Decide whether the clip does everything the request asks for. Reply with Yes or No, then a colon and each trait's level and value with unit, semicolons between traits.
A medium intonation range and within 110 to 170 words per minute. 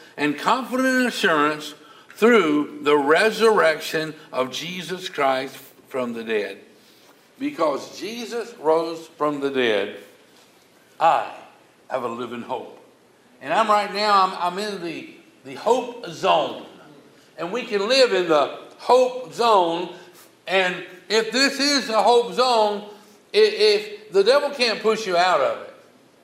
No: wide, 7.5 semitones; slow, 135 wpm